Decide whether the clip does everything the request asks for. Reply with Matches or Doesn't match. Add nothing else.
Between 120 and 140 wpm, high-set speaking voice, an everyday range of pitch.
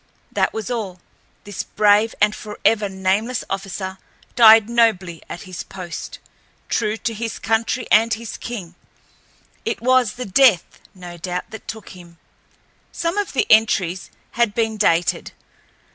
Matches